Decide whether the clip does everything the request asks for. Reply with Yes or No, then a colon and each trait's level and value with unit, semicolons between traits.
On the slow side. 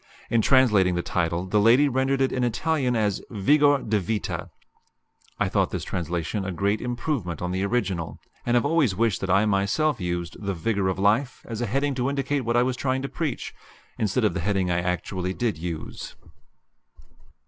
No: average, 190 wpm